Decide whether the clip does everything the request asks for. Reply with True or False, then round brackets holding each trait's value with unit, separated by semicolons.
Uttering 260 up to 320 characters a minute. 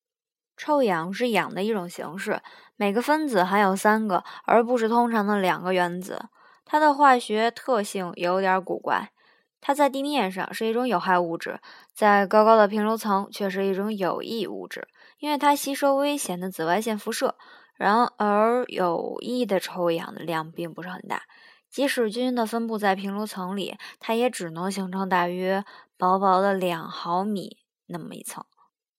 False (250 characters per minute)